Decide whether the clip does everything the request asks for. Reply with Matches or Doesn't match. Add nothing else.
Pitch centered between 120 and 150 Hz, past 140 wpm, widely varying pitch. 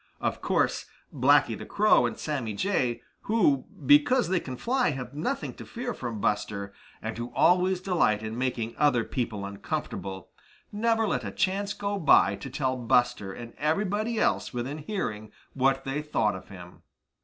Matches